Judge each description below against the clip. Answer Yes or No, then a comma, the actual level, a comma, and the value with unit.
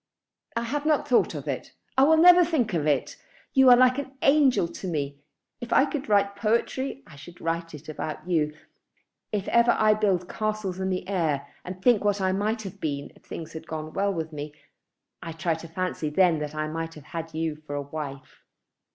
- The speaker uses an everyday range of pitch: No, wide, 6.4 semitones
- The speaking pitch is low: No, medium, 185 Hz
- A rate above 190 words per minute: Yes, fast, 205 wpm